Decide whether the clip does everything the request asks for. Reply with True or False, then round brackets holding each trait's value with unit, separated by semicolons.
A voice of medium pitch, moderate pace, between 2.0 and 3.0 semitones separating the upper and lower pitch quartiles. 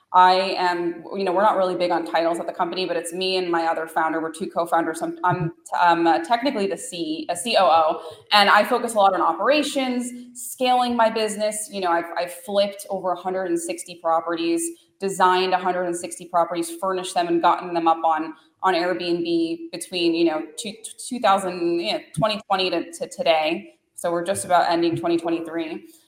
False (180 Hz; 175 wpm; 3.6 semitones)